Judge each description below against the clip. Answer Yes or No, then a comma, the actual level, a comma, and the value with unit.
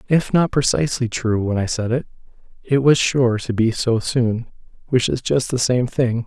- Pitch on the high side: No, low, 120 Hz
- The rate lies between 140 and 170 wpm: No, average, 200 wpm